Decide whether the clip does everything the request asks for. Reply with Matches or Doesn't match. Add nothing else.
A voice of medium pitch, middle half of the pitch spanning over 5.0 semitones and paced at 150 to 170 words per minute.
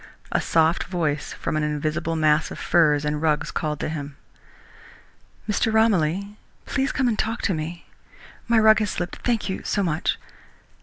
Matches